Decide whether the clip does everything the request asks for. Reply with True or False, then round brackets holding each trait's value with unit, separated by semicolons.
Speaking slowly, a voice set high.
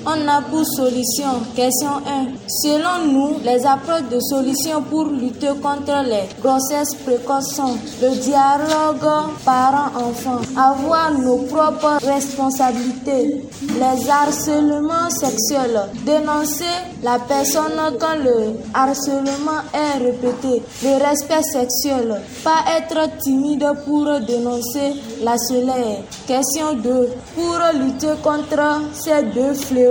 True (110 wpm; 275 Hz)